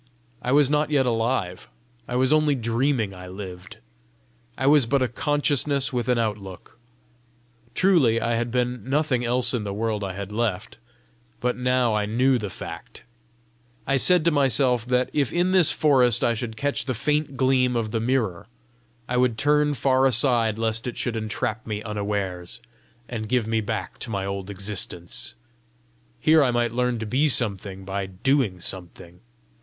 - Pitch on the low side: Yes, low, 120 Hz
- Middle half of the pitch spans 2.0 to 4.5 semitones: Yes, average, 4.0 semitones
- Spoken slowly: No, average, 170 wpm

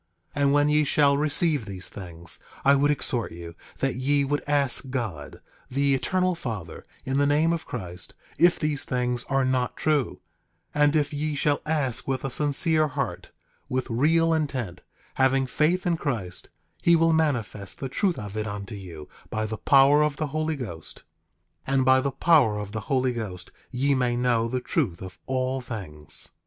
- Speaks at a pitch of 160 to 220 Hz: No, low, 135 Hz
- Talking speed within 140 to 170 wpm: No, average, 180 wpm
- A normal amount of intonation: Yes, average, 4.8 semitones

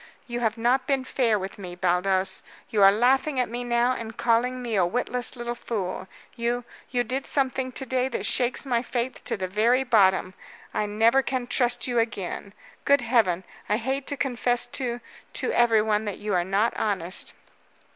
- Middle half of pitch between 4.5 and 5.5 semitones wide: No, average, 3.3 semitones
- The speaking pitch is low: No, high, 235 Hz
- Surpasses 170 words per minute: Yes, average, 185 wpm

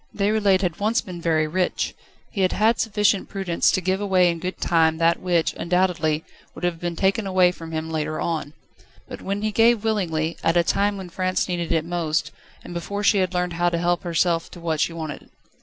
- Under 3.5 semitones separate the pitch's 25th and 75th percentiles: Yes, average, 2.7 semitones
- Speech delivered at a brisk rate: Yes, fast, 210 wpm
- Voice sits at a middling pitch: Yes, medium, 175 Hz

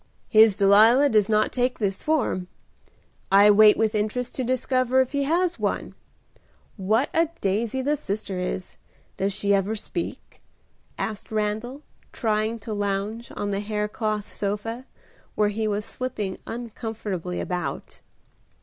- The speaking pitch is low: No, high, 215 Hz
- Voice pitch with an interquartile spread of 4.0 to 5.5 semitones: No, average, 3.3 semitones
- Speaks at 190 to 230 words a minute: No, slow, 135 wpm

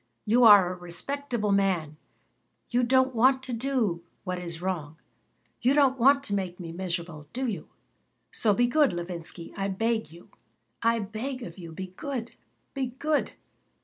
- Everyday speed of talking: Yes, average, 165 wpm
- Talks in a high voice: Yes, high, 210 Hz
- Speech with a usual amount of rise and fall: No, wide, 6.3 semitones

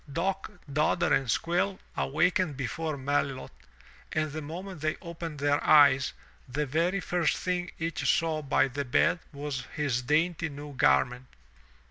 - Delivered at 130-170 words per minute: Yes, average, 140 wpm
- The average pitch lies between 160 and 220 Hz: No, medium, 150 Hz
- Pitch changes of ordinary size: Yes, average, 3.2 semitones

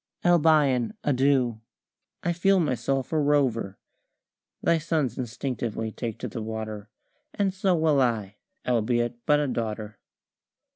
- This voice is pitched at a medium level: No, low, 125 Hz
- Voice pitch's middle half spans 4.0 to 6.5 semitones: Yes, average, 5.1 semitones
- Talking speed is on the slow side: Yes, slow, 125 wpm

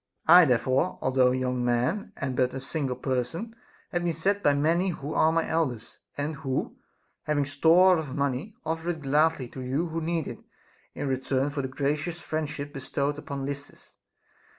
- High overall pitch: No, medium, 145 Hz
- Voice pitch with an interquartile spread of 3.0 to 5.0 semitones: Yes, average, 3.6 semitones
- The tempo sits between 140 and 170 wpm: No, average, 180 wpm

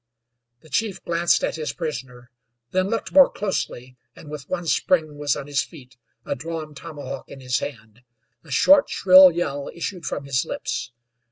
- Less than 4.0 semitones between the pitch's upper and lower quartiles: No, average, 4.6 semitones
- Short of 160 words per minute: No, average, 170 wpm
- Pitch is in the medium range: Yes, medium, 150 Hz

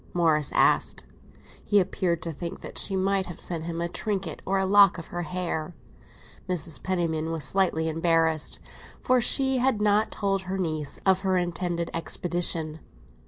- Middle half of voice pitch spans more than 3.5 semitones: No, average, 2.8 semitones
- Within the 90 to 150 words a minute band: No, average, 165 wpm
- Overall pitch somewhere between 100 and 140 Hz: No, medium, 175 Hz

